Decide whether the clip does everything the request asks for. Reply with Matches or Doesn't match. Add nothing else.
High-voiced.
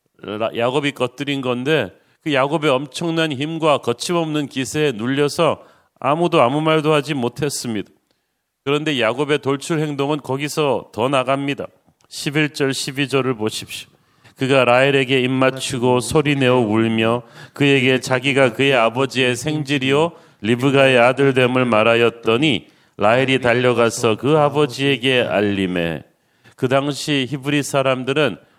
Doesn't match